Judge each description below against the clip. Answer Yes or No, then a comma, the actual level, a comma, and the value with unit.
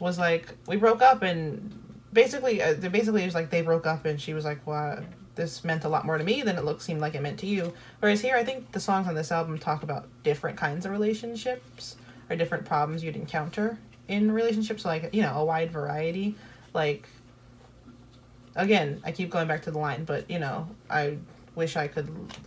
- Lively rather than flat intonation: No, average, 4.8 semitones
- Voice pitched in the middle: Yes, medium, 165 Hz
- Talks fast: Yes, fast, 215 wpm